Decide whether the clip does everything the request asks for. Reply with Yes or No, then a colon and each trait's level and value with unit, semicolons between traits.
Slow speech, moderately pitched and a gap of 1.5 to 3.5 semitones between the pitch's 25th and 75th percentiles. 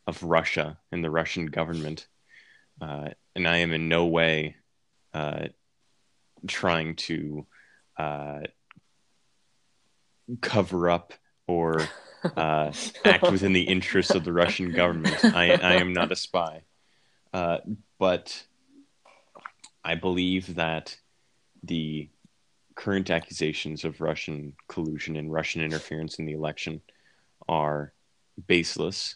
No: slow, 110 wpm; very low, 80 Hz; narrow, 2.5 semitones